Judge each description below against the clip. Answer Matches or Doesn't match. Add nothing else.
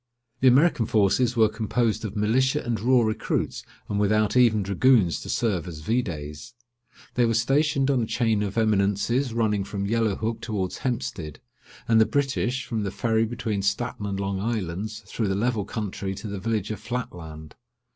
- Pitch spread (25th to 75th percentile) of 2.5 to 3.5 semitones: Matches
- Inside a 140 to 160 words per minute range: Doesn't match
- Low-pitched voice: Matches